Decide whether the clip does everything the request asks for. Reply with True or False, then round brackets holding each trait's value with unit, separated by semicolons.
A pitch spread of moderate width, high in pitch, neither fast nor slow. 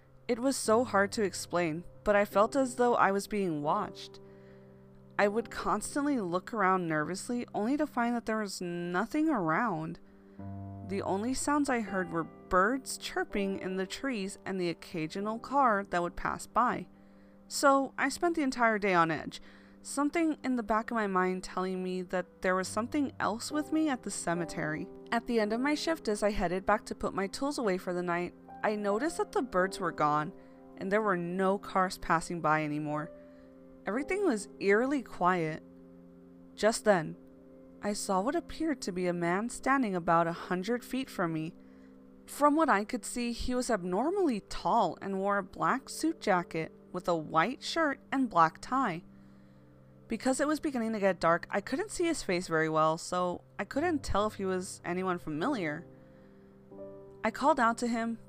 False (7.0 semitones; 195 Hz; 185 wpm)